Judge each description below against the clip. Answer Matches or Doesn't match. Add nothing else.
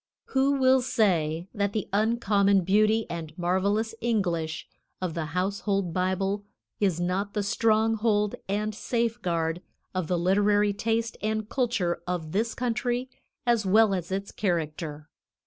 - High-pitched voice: Matches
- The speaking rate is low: Matches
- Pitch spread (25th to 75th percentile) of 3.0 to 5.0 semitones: Matches